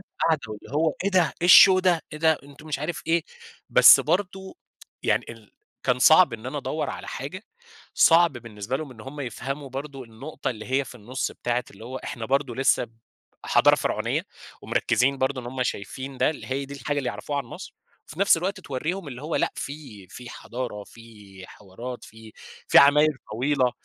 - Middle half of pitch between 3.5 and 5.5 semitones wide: Yes, average, 4.0 semitones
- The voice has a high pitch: No, low, 135 Hz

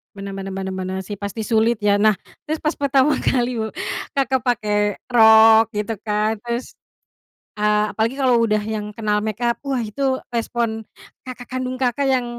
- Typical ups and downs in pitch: Yes, average, 3.1 semitones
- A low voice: No, high, 225 Hz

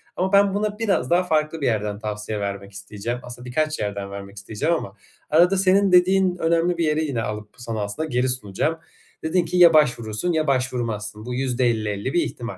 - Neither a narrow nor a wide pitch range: No, wide, 8.1 semitones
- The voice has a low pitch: Yes, low, 125 Hz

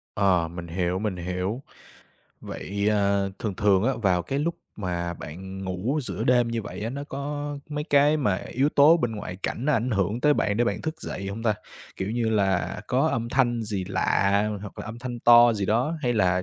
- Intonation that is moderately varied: Yes, average, 4.9 semitones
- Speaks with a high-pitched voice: No, low, 110 Hz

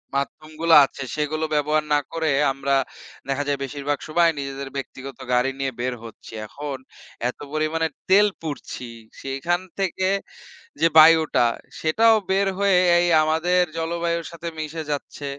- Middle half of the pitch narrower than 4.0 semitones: Yes, average, 3.4 semitones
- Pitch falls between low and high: Yes, medium, 155 Hz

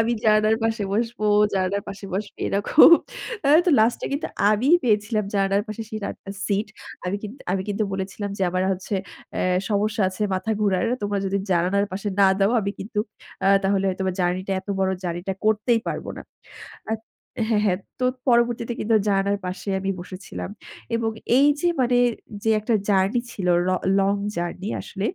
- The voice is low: No, high, 200 Hz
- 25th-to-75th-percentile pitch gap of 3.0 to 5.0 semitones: No, narrow, 2.4 semitones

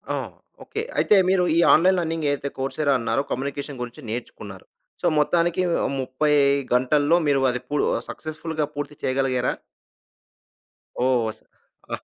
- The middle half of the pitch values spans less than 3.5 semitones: No, average, 3.8 semitones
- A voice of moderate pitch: Yes, medium, 145 Hz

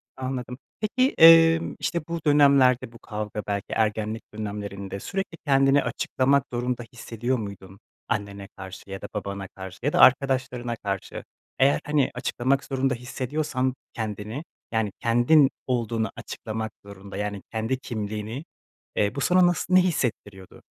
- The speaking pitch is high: No, low, 120 Hz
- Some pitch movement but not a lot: Yes, average, 4.8 semitones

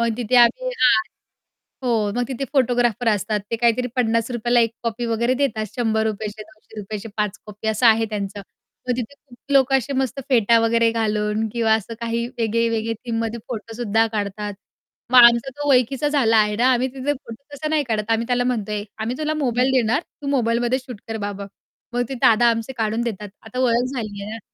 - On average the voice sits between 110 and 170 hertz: No, high, 230 Hz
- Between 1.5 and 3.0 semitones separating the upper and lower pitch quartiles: Yes, narrow, 2.4 semitones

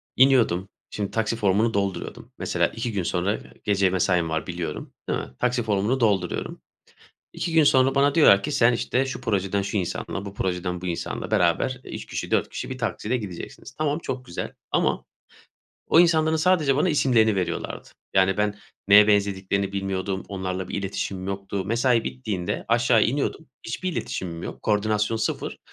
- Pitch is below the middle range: Yes, low, 105 Hz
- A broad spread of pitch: No, average, 4.8 semitones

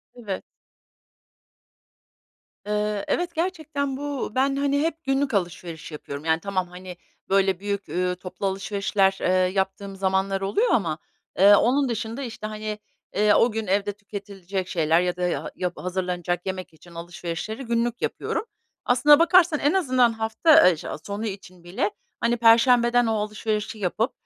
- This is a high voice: Yes, high, 205 Hz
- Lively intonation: No, average, 4.8 semitones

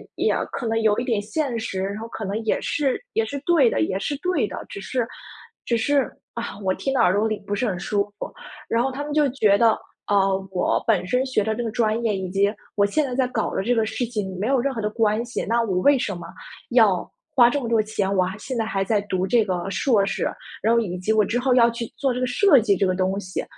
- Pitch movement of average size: Yes, average, 3.8 semitones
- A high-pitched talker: Yes, high, 220 Hz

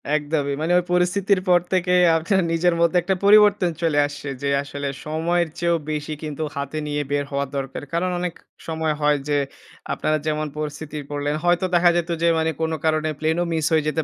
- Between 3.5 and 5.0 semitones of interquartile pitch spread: No, average, 2.8 semitones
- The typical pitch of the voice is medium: Yes, medium, 160 Hz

